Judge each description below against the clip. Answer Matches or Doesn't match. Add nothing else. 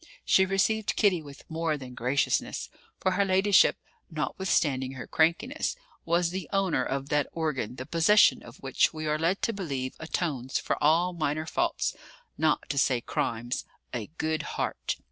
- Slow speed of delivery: Doesn't match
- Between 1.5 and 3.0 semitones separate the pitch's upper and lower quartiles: Doesn't match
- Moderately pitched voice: Matches